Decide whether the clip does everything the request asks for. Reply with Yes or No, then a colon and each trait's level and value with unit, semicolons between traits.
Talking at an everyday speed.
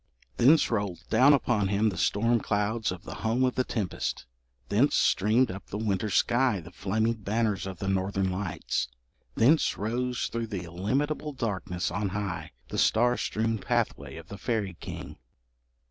Yes: average, 160 wpm